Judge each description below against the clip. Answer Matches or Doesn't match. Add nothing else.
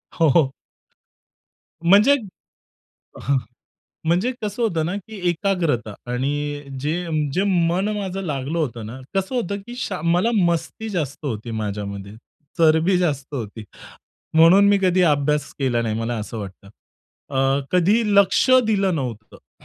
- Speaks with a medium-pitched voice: Matches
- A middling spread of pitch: Doesn't match